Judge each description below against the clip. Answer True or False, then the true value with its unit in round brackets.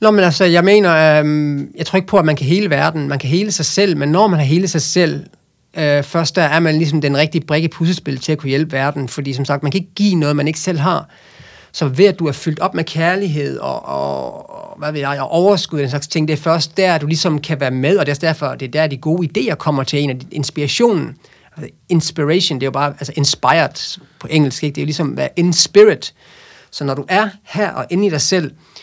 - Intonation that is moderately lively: True (3.3 semitones)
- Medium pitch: True (155 Hz)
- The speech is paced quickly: True (270 wpm)